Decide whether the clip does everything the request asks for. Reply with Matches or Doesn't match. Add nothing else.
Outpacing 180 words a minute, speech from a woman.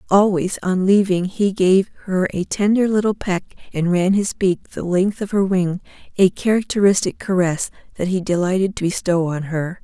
Doesn't match